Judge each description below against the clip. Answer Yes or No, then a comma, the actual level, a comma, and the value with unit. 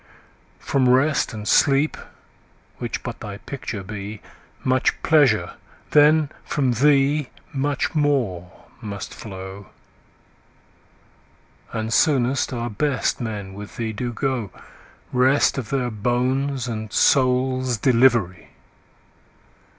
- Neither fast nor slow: No, slow, 105 wpm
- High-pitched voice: No, low, 125 Hz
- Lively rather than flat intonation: No, average, 4.2 semitones